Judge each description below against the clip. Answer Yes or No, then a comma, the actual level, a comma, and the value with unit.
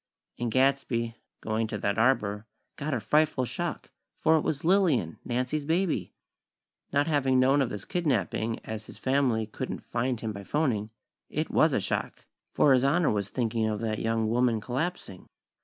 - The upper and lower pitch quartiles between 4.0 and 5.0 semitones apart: Yes, average, 4.5 semitones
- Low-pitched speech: Yes, low, 125 Hz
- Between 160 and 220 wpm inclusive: Yes, average, 170 wpm